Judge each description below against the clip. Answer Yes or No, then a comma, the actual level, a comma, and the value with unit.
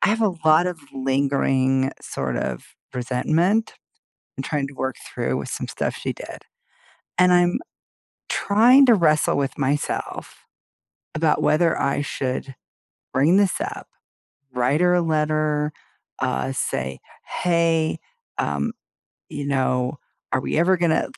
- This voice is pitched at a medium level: Yes, medium, 150 Hz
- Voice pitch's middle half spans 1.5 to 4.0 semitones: No, average, 4.7 semitones